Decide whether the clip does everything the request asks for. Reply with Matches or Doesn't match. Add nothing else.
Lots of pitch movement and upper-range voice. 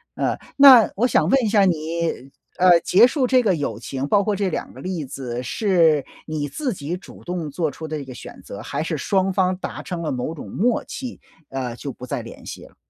Doesn't match